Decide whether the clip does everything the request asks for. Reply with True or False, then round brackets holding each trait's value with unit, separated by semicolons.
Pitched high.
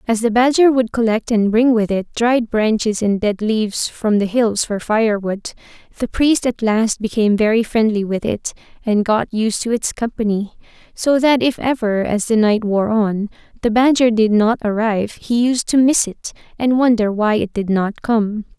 True (220 Hz)